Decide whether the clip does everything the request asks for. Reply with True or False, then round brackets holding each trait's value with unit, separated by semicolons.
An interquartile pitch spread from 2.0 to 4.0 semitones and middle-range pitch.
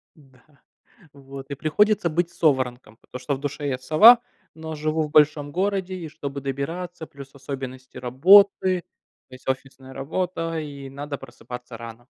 True (3.7 semitones; 145 Hz)